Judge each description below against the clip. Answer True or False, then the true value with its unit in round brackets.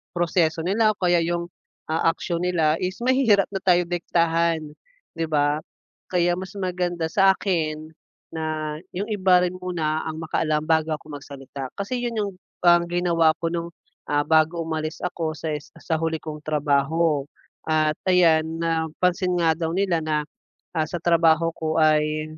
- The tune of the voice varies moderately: False (2.2 semitones)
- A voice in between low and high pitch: True (165 Hz)